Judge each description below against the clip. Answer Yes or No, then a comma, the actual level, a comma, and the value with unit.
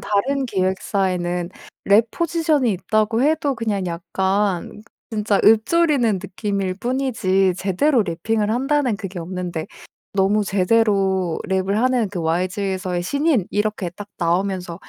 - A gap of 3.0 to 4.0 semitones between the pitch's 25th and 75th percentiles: Yes, average, 3.6 semitones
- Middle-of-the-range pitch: No, high, 200 Hz